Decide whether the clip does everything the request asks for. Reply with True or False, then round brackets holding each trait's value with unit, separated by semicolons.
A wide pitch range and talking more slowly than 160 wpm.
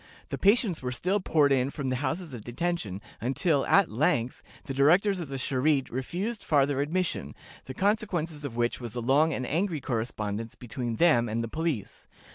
False (5.8 semitones; 180 wpm)